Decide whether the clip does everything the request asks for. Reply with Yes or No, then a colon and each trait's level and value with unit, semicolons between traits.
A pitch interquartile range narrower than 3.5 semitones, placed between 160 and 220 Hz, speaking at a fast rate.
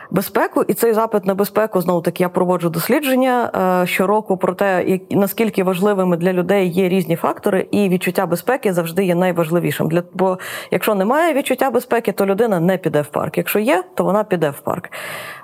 Yes: average, 3.0 semitones; high, 190 Hz; fast, 180 wpm